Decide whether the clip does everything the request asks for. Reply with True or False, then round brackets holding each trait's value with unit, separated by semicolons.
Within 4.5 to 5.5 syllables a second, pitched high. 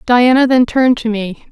True (5.1 syllables/s; 240 Hz)